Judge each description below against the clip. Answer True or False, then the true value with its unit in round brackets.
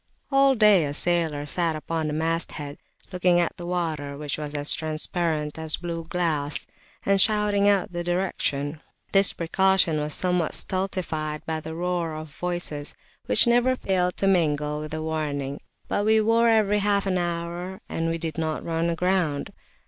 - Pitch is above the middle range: False (170 Hz)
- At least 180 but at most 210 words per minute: False (165 wpm)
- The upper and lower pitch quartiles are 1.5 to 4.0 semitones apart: True (3.5 semitones)